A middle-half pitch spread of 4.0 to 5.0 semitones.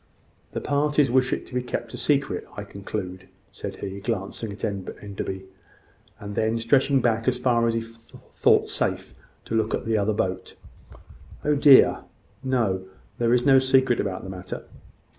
Yes: average, 4.6 semitones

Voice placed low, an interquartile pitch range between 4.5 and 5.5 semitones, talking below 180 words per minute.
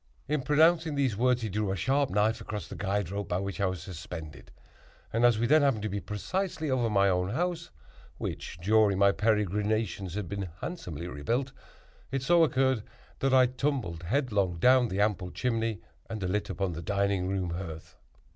No: low, 105 Hz; average, 5.2 semitones; average, 185 wpm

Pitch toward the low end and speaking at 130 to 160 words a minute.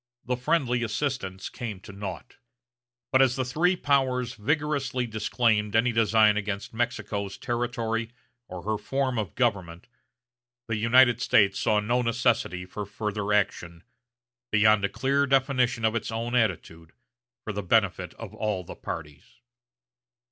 Yes: low, 115 Hz; average, 140 wpm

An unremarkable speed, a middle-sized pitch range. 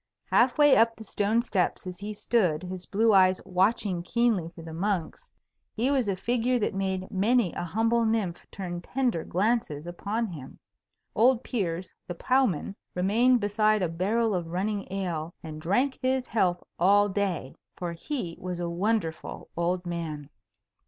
Yes: average, 160 wpm; average, 4.6 semitones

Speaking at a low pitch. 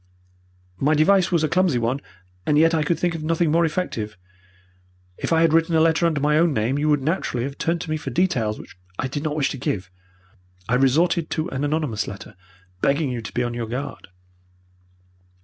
No: medium, 150 Hz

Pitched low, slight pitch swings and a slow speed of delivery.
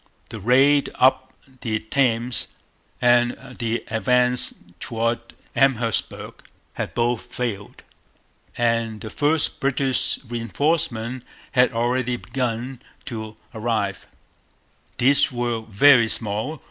Yes: low, 120 Hz; narrow, 2.2 semitones; slow, 95 wpm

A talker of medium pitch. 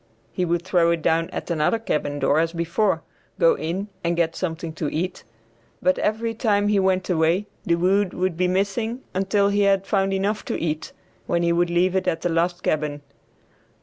Yes: medium, 180 Hz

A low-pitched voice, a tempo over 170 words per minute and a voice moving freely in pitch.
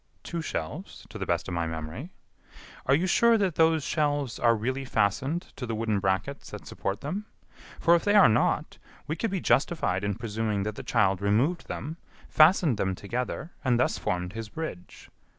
Yes: low, 125 Hz; average, 185 wpm; wide, 8.0 semitones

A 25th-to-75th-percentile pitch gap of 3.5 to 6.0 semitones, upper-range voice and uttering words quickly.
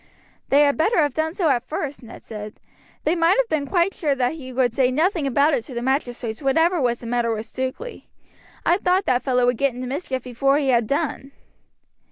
Yes: average, 4.3 semitones; very high, 275 Hz; fast, 220 wpm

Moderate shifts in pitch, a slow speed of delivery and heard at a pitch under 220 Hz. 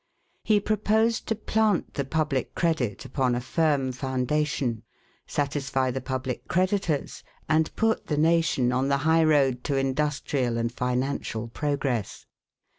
Yes: average, 3.9 semitones; slow, 130 wpm; medium, 140 Hz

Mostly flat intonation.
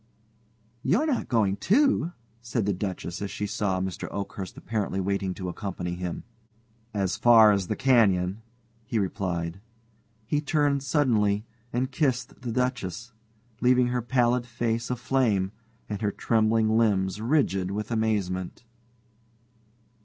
No: average, 4.3 semitones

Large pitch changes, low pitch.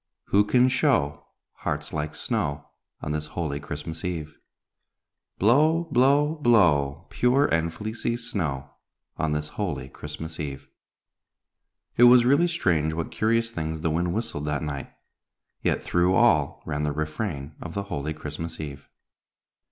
Yes: wide, 7.5 semitones; very low, 80 Hz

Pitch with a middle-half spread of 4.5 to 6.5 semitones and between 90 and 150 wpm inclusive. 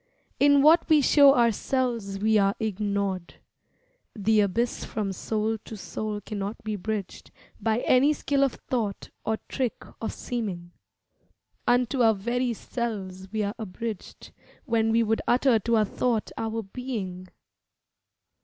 No: average, 3.2 semitones; slow, 135 wpm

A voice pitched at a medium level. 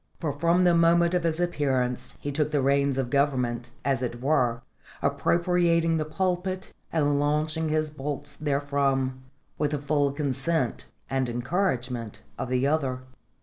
Yes: medium, 145 Hz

